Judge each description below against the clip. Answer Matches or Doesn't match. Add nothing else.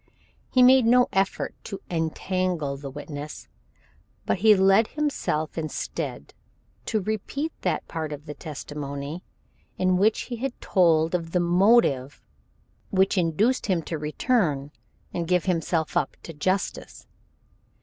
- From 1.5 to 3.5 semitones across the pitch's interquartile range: Doesn't match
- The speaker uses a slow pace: Matches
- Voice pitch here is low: Doesn't match